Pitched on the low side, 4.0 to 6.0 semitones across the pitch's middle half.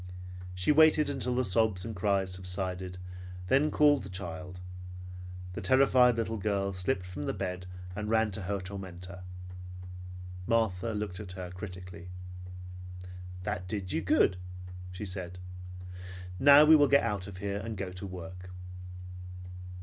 No: very low, 95 Hz; average, 3.6 semitones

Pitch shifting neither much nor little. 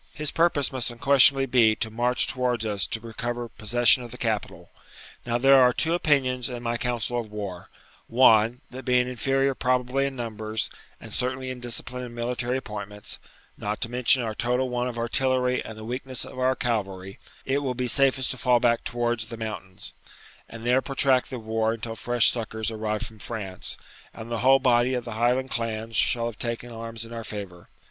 No: narrow, 2.3 semitones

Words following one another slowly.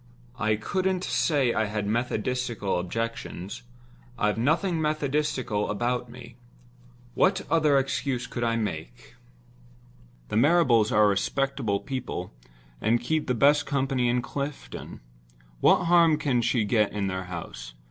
Yes: slow, 125 wpm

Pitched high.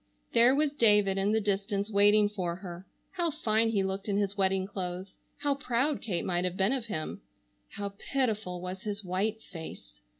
Yes: high, 200 Hz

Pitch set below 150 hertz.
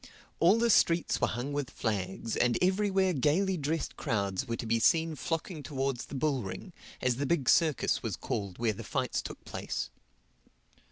Yes: medium, 140 Hz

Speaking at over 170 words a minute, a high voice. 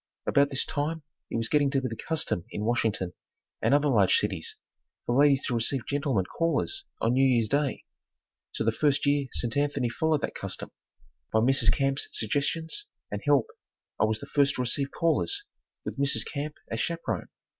No: average, 180 wpm; medium, 140 Hz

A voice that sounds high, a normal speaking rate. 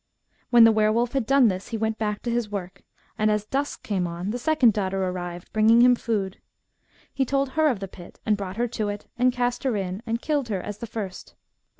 No: high, 220 Hz; fast, 235 wpm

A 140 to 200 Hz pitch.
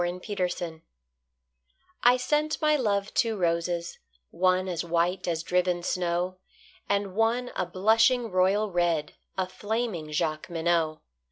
Yes: medium, 185 Hz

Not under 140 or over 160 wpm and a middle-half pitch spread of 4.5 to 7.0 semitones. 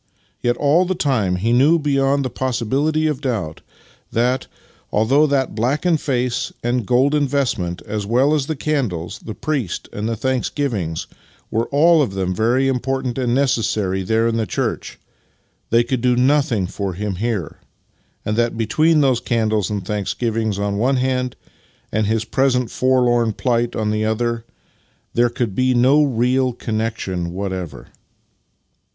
No: average, 155 wpm; average, 3.8 semitones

